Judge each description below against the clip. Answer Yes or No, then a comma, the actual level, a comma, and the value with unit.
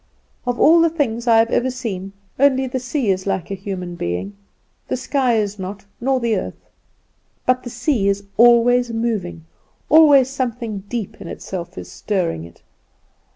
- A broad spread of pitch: No, average, 4.6 semitones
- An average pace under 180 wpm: Yes, average, 165 wpm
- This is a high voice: Yes, high, 230 Hz